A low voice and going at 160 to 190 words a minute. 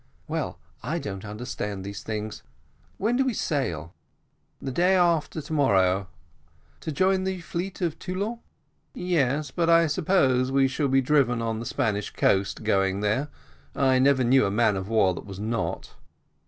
Yes: low, 130 Hz; average, 165 wpm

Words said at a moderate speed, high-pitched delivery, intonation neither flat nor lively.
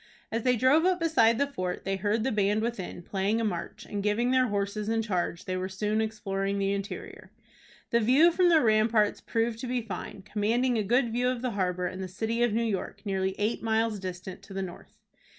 No: fast, 220 wpm; high, 215 Hz; average, 3.3 semitones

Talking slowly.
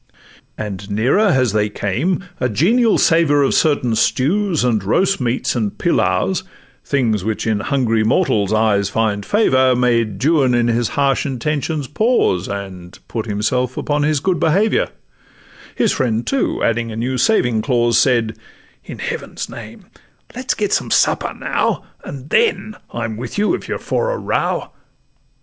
No: average, 155 wpm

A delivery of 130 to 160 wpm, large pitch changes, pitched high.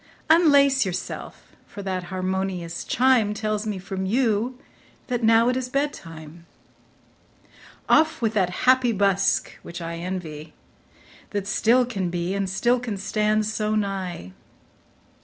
No: slow, 135 wpm; average, 4.6 semitones; high, 205 Hz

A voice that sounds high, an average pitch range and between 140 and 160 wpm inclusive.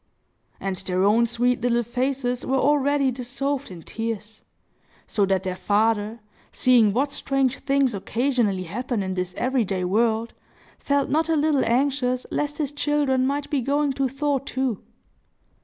Yes: very high, 250 Hz; average, 4.2 semitones; average, 155 wpm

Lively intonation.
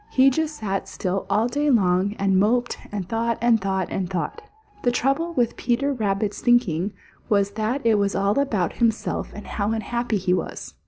No: average, 3.7 semitones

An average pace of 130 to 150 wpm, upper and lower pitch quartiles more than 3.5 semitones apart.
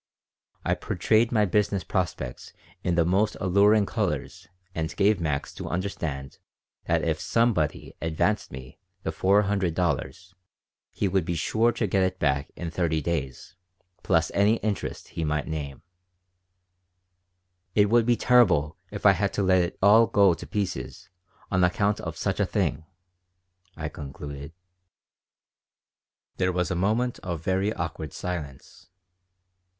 Yes: average, 145 wpm; average, 4.4 semitones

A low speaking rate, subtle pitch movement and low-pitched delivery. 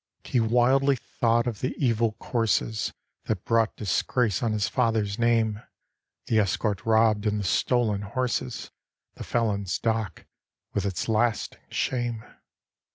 Yes: slow, 130 wpm; narrow, 2.2 semitones; low, 110 Hz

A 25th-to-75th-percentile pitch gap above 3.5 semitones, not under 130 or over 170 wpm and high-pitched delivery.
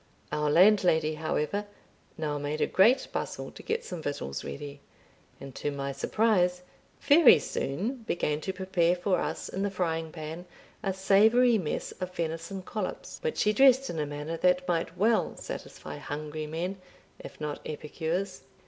No: average, 4.5 semitones; average, 155 wpm; medium, 175 Hz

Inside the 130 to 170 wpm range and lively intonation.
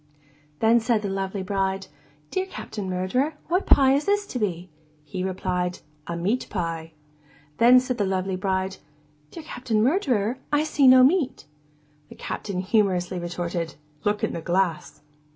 Yes: average, 150 wpm; wide, 5.7 semitones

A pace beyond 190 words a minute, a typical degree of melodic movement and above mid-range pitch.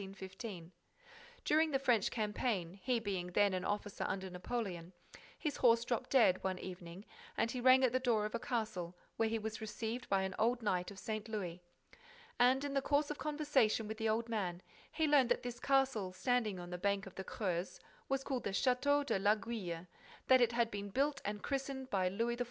Yes: average, 200 wpm; average, 4.8 semitones; high, 220 Hz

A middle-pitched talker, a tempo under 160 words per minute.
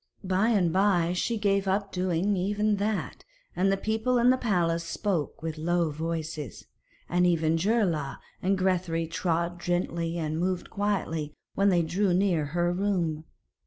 Yes: medium, 180 Hz; average, 150 wpm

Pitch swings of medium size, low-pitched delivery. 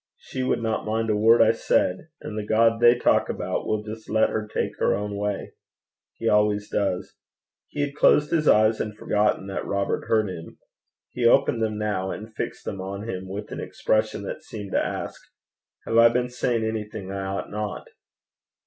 No: narrow, 1.8 semitones; low, 105 Hz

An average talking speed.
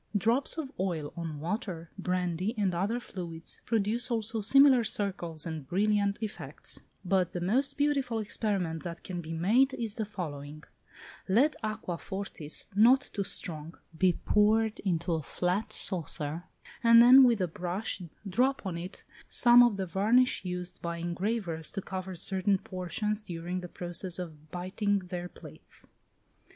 Yes: average, 150 wpm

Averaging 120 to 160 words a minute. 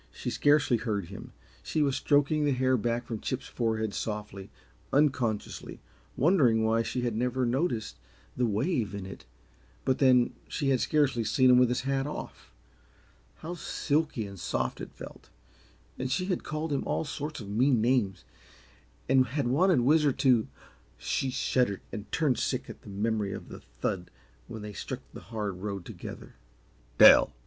No: average, 170 wpm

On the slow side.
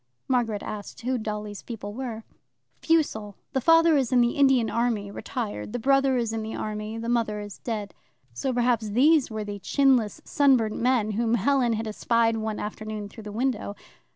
No: average, 180 wpm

